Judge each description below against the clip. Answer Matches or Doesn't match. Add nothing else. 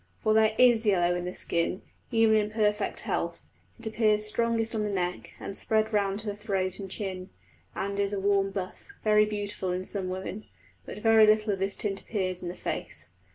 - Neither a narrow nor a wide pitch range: Doesn't match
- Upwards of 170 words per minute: Matches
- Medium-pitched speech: Doesn't match